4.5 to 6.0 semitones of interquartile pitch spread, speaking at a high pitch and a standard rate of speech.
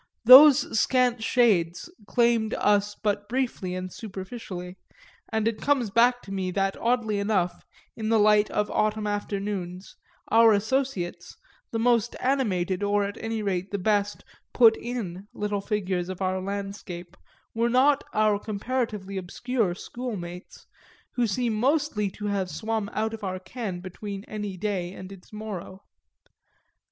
No: average, 3.3 semitones; high, 210 Hz; average, 145 wpm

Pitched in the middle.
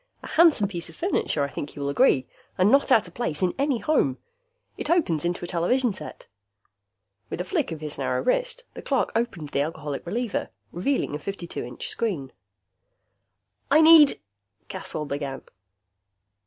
Yes: medium, 180 Hz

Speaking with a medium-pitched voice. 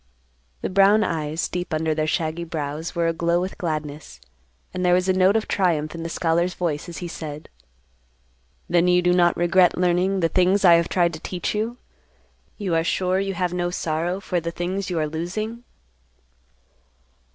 Yes: medium, 175 Hz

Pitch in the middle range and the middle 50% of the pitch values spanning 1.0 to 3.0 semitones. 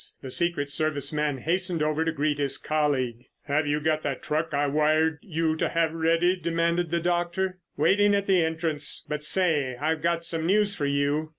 Yes: medium, 160 Hz; narrow, 2.5 semitones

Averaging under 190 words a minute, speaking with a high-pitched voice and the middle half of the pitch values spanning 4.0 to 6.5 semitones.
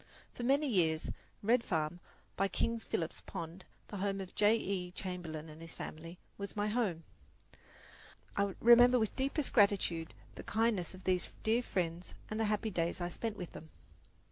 Yes: average, 170 wpm; high, 195 Hz; average, 4.7 semitones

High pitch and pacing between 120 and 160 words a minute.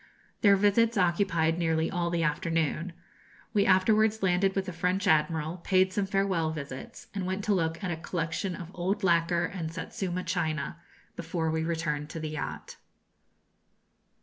No: medium, 175 Hz; average, 155 wpm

